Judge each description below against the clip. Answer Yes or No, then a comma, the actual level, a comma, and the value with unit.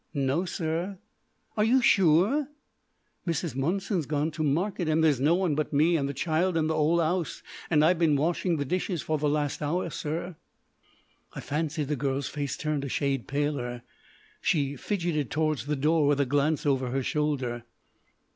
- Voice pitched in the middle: Yes, medium, 155 Hz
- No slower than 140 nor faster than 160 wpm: No, average, 175 wpm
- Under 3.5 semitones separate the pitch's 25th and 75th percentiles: Yes, average, 3.1 semitones